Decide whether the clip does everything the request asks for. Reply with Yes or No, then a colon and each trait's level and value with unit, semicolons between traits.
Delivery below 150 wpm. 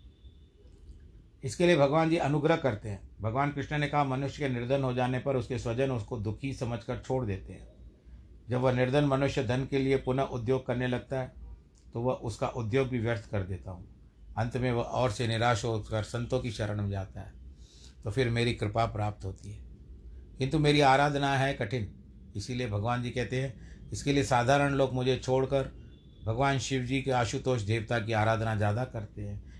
No: fast, 190 wpm